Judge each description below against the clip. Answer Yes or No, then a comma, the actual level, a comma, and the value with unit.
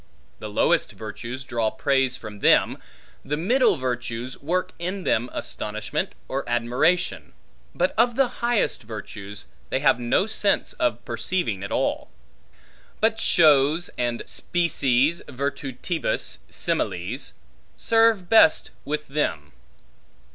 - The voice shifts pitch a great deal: Yes, wide, 7.0 semitones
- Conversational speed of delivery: No, slow, 115 wpm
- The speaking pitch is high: No, low, 135 Hz